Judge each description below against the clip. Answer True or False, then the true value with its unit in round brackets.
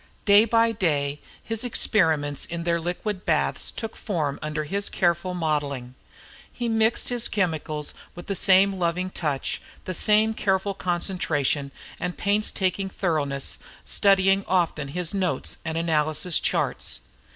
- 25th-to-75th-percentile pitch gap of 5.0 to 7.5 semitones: False (4.5 semitones)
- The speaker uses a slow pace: True (130 wpm)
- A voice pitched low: False (180 Hz)